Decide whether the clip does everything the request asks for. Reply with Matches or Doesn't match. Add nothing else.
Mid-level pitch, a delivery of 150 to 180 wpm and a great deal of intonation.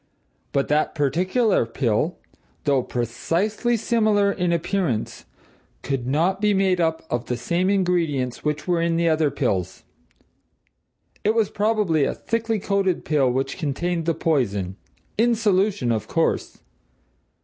Doesn't match